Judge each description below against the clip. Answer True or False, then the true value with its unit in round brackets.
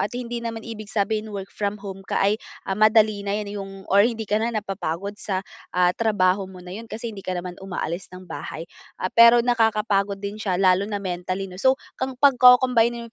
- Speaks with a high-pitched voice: True (205 Hz)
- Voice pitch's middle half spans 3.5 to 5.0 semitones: False (2.9 semitones)